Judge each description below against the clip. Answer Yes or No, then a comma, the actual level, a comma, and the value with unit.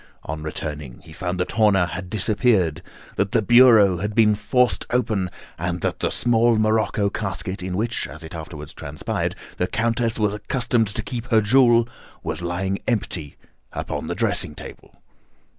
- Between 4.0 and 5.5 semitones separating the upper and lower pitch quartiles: Yes, average, 4.6 semitones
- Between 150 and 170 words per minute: Yes, average, 160 wpm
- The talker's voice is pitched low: Yes, low, 105 Hz